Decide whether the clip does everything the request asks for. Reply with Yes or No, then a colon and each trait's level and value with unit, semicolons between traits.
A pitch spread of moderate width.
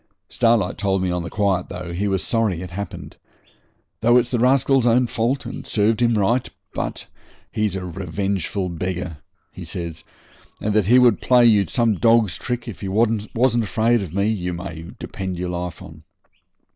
Yes: average, 4.3 semitones